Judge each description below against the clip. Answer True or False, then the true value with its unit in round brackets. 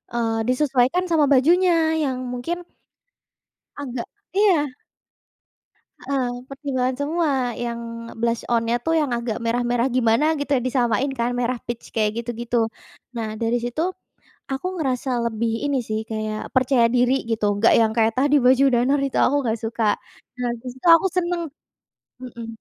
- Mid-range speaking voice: False (250 Hz)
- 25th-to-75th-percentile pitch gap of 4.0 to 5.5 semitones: False (3.3 semitones)